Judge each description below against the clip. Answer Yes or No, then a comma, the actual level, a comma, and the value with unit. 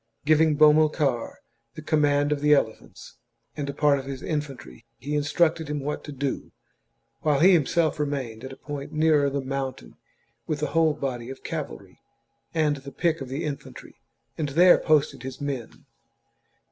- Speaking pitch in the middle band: Yes, medium, 145 Hz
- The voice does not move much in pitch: Yes, narrow, 2.1 semitones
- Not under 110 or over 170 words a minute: Yes, average, 165 wpm